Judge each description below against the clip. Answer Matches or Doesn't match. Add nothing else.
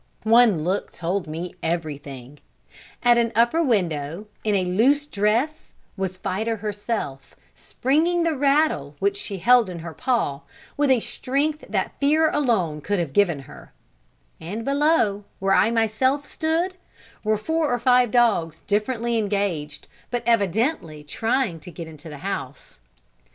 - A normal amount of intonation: Doesn't match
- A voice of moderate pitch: Doesn't match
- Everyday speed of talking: Matches